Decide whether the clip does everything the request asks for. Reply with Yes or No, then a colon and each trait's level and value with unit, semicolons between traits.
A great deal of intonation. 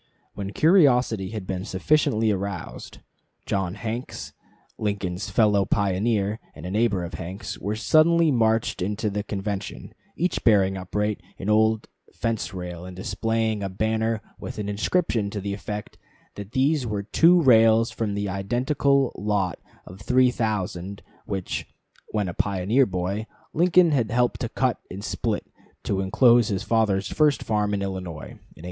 No: average, 3.1 semitones